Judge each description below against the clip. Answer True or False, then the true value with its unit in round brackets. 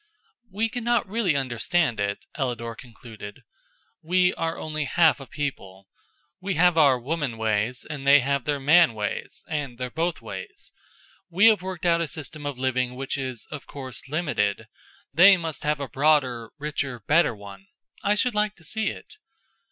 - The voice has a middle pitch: True (145 Hz)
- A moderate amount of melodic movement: False (5.7 semitones)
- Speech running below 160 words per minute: False (165 wpm)